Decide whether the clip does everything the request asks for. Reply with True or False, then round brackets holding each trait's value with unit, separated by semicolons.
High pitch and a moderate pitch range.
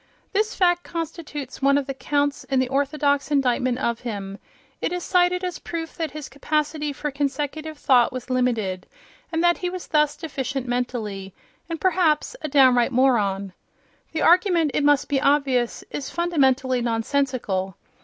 True (280 Hz; 4.0 semitones)